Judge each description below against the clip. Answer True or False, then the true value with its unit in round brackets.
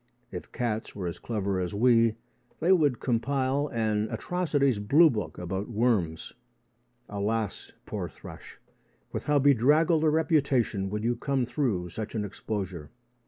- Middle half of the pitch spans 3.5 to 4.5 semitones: False (5.5 semitones)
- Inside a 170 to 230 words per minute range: False (140 wpm)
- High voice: False (115 Hz)